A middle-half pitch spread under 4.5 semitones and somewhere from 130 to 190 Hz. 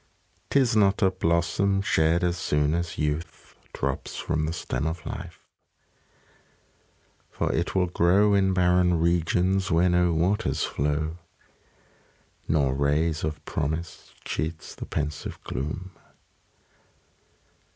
No: average, 2.8 semitones; very low, 85 Hz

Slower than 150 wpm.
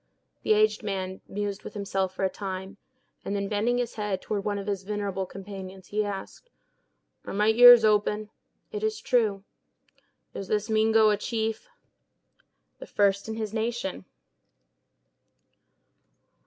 Yes: average, 140 wpm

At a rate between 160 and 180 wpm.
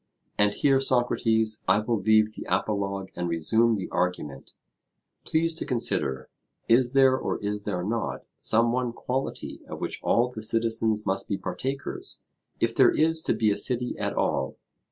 Yes: average, 165 wpm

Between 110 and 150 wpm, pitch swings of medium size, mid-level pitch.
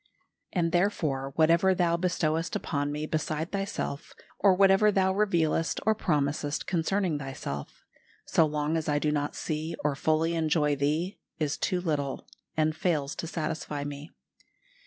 Yes: average, 145 wpm; average, 3.1 semitones; medium, 160 Hz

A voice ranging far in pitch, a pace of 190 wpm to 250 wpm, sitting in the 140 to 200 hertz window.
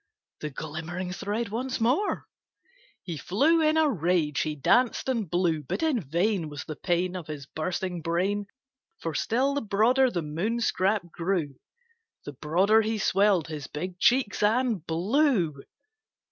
No: wide, 5.9 semitones; average, 150 wpm; medium, 185 Hz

